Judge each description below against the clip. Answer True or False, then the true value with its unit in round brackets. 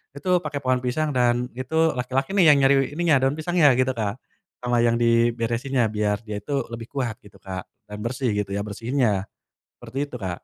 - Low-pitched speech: True (125 Hz)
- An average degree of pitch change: True (3.2 semitones)